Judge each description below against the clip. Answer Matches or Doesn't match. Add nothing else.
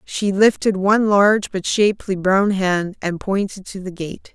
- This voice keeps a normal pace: Matches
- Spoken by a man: Doesn't match